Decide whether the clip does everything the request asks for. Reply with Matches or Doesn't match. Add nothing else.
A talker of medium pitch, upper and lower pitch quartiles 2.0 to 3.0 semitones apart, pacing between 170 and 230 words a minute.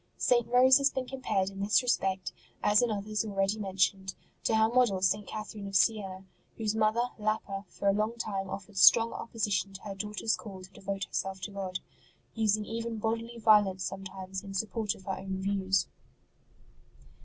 Doesn't match